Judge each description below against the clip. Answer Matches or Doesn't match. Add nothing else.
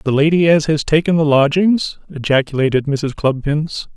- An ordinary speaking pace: Matches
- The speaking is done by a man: Matches